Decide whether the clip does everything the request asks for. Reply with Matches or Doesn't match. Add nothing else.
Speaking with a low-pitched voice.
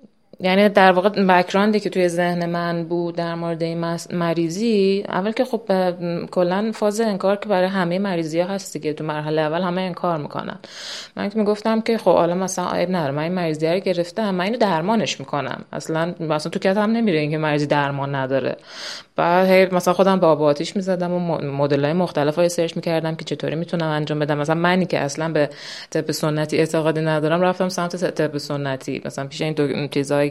Doesn't match